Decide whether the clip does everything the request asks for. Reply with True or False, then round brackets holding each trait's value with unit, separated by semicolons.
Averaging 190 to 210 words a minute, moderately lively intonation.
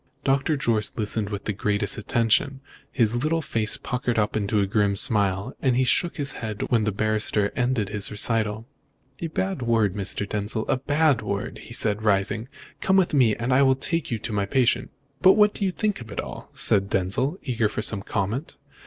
True (195 wpm; 4.2 semitones)